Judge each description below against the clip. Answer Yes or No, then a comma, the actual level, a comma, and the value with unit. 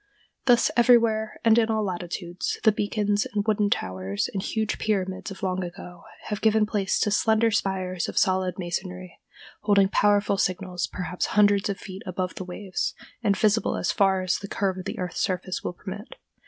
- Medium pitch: No, high, 195 Hz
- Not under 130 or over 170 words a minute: No, average, 180 wpm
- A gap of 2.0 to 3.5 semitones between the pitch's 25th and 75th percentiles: Yes, narrow, 2.4 semitones